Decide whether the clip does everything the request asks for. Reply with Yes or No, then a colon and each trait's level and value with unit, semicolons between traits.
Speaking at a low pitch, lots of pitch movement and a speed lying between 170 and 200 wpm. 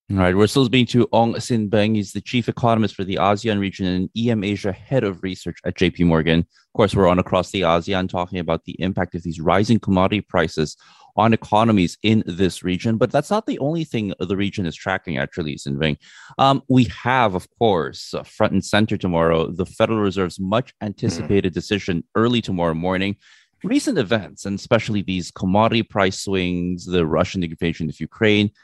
No: low, 100 Hz; average, 3.7 semitones; average, 190 wpm